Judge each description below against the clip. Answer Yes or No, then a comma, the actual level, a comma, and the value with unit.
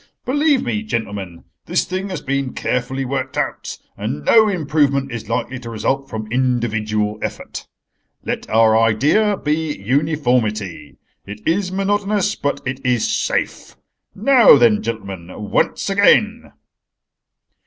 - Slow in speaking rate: Yes, slow, 125 wpm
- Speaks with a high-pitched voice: No, low, 135 Hz